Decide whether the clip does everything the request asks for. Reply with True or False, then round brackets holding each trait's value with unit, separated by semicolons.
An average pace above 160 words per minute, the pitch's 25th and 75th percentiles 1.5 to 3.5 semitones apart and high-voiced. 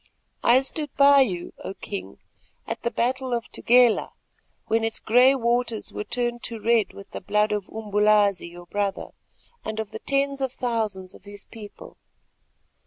True (170 wpm; 3.2 semitones; 225 Hz)